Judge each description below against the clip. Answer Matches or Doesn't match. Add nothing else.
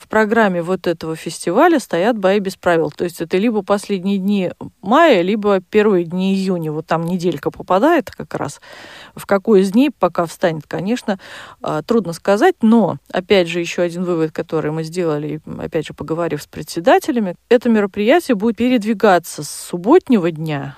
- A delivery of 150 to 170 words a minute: Matches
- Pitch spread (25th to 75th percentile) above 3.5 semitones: Matches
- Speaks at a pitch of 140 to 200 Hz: Matches